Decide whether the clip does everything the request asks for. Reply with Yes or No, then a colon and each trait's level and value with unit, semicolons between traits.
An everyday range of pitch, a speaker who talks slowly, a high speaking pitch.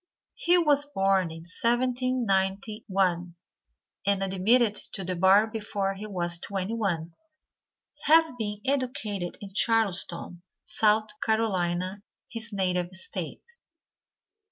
Yes: average, 3.7 semitones; slow, 105 wpm; high, 200 Hz